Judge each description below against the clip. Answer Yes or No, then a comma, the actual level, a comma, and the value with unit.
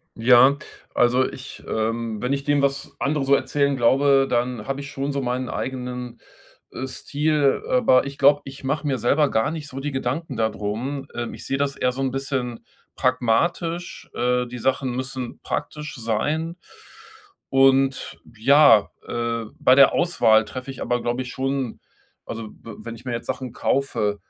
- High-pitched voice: No, low, 130 Hz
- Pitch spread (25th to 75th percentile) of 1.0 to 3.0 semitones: Yes, narrow, 2.5 semitones